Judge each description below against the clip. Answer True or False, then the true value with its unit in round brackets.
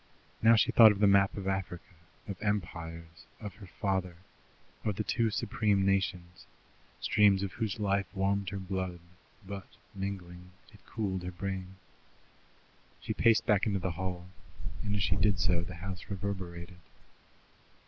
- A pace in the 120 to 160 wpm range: True (150 wpm)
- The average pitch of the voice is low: True (95 Hz)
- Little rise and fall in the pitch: True (2.0 semitones)